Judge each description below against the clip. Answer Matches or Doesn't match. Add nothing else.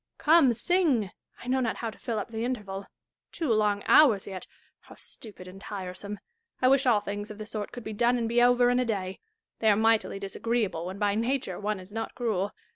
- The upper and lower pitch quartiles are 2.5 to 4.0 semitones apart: Matches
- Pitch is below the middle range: Doesn't match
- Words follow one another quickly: Matches